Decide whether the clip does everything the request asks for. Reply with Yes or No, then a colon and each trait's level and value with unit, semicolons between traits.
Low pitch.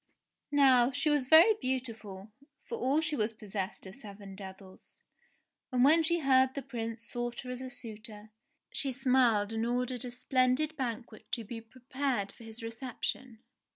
No: high, 245 Hz